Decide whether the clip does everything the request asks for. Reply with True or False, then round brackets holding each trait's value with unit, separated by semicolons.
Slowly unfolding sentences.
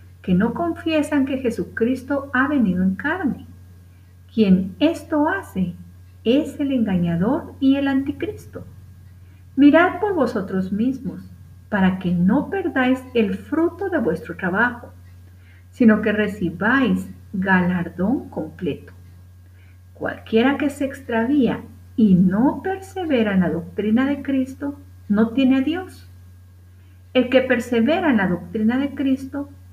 True (120 wpm)